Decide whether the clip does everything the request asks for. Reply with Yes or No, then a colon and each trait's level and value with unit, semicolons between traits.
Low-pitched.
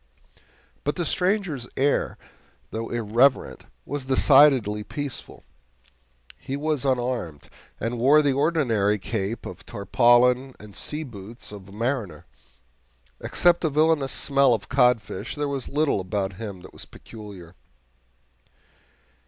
Yes: low, 125 Hz